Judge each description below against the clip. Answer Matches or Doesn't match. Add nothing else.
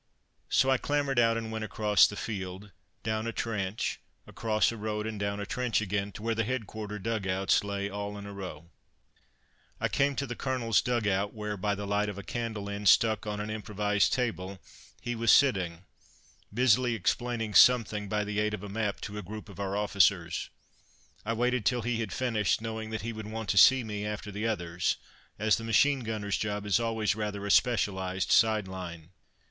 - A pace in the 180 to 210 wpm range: Matches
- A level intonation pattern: Matches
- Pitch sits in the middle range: Doesn't match